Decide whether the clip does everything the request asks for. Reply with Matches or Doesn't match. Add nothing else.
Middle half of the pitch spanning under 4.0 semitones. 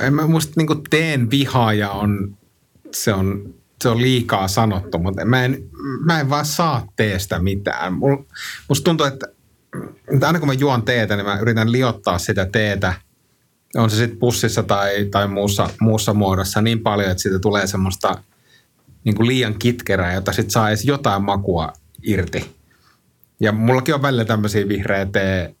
Doesn't match